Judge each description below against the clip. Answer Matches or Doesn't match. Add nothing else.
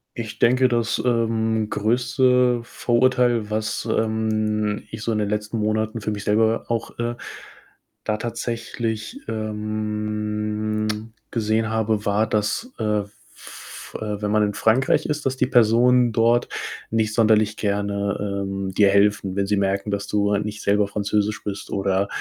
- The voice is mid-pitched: Doesn't match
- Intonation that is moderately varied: Doesn't match